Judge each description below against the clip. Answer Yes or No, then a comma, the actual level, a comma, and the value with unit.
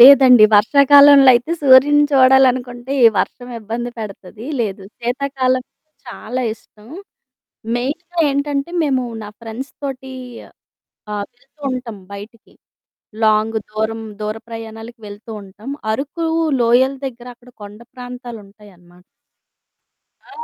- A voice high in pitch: Yes, high, 245 Hz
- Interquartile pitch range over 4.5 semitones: No, average, 3.5 semitones